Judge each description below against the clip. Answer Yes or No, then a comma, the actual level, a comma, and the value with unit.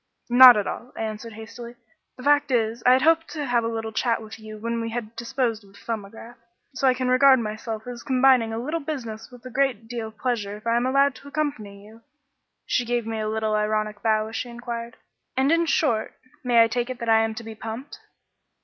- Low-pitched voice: No, high, 235 Hz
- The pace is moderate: No, fast, 230 wpm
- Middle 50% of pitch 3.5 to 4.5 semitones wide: No, narrow, 2.6 semitones